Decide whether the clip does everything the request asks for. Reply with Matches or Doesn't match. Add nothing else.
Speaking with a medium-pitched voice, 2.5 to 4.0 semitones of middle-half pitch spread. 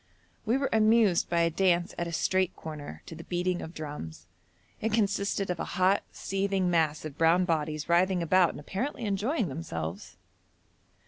Matches